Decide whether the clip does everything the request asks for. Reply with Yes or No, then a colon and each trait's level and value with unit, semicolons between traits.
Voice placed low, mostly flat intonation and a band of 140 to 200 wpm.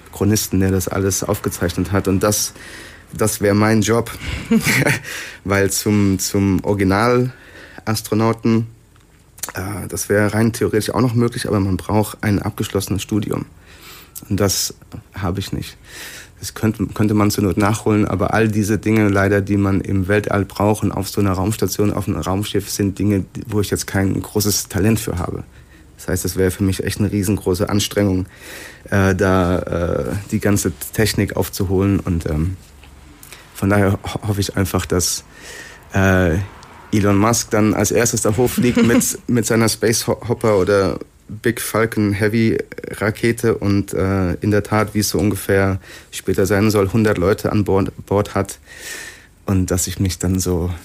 Yes: low, 100 Hz; narrow, 2.0 semitones; average, 160 wpm